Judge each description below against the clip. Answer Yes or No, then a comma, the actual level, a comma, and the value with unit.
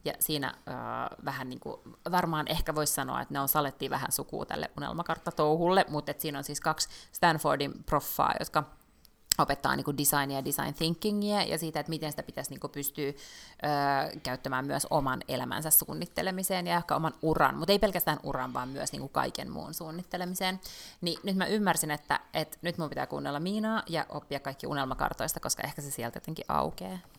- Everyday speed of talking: No, fast, 180 wpm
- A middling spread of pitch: Yes, average, 3.6 semitones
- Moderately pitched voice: Yes, medium, 155 Hz